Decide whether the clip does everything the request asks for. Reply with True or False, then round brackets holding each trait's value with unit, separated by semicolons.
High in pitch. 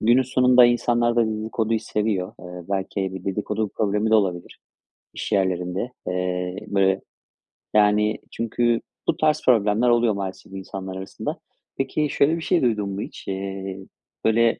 False (105 Hz)